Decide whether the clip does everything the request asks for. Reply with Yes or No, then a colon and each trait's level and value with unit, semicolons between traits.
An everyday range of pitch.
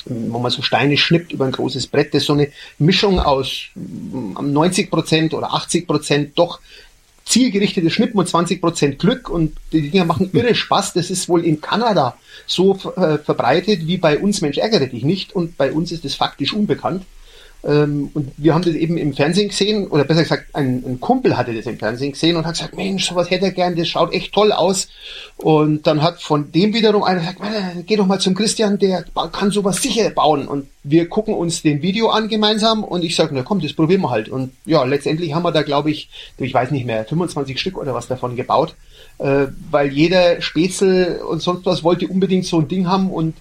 Yes: average, 4.4 semitones